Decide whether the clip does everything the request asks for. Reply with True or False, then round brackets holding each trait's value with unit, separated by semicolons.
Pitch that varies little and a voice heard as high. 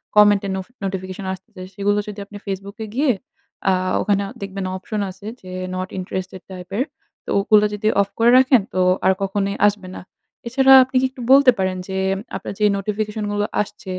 True (1.9 semitones; 200 Hz)